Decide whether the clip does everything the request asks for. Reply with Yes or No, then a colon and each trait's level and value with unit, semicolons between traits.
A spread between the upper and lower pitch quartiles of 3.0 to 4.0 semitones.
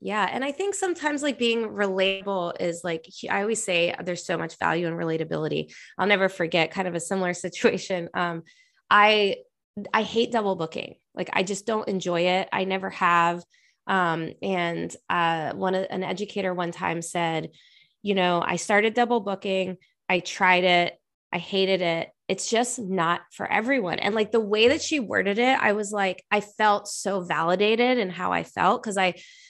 Yes: average, 3.6 semitones